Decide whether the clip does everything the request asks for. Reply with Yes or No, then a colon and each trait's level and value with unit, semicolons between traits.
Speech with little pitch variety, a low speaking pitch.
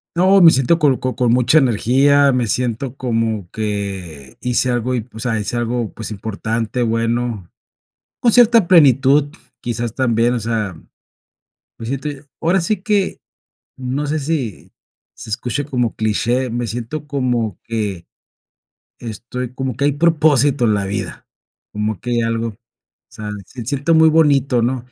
No: average, 3.9 semitones; low, 125 Hz